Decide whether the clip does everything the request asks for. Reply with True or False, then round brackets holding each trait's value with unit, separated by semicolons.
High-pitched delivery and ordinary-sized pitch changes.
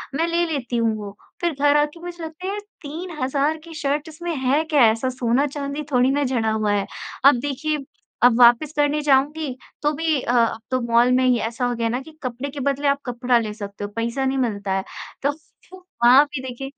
True (270 Hz; 3.7 semitones)